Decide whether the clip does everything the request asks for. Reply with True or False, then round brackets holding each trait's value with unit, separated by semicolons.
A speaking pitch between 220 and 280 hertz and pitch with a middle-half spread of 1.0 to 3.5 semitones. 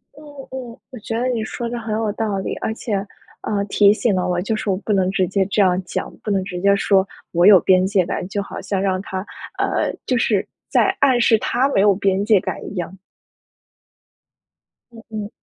False (200 Hz; 2.7 semitones)